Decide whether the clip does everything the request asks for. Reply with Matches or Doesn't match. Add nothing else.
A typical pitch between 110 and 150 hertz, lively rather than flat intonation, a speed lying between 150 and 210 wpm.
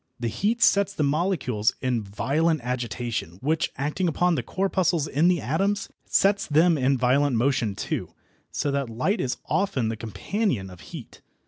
Matches